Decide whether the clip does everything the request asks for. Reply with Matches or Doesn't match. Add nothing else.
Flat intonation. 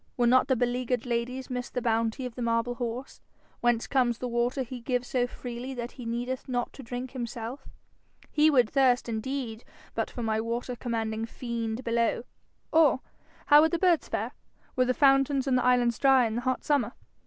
Matches